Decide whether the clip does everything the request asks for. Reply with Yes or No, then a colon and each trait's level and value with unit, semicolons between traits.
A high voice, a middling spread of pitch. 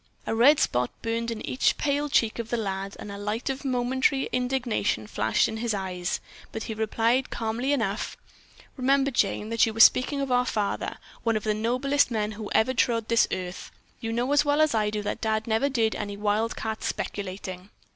Yes: high, 225 Hz; average, 3.3 semitones